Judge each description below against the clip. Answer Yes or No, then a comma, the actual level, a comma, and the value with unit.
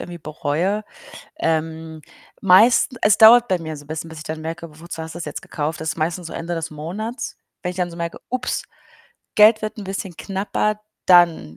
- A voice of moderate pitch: Yes, medium, 170 Hz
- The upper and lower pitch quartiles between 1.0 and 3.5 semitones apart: No, average, 4.0 semitones